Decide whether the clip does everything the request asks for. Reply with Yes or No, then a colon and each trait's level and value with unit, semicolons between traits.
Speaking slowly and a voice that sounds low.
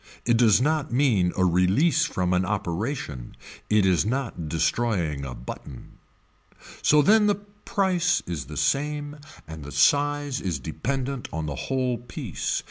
No: average, 145 wpm; low, 120 Hz